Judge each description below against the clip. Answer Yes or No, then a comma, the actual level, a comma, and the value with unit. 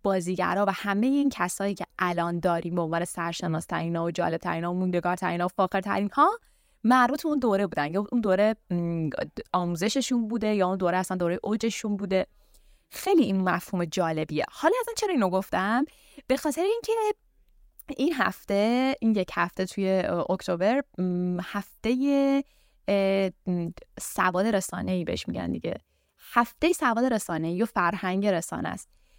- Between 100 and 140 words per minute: No, average, 150 wpm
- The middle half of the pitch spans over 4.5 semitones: Yes, wide, 5.4 semitones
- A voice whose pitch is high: Yes, high, 195 Hz